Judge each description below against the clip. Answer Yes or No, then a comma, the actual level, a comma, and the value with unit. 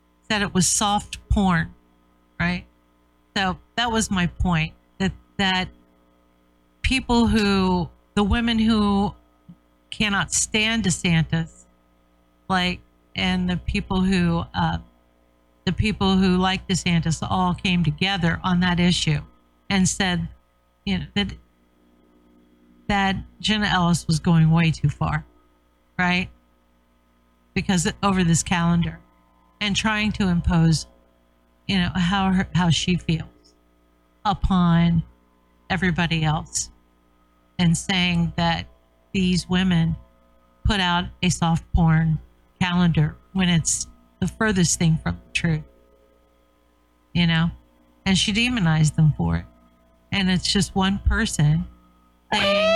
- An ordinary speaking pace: No, slow, 115 wpm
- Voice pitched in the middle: Yes, medium, 160 Hz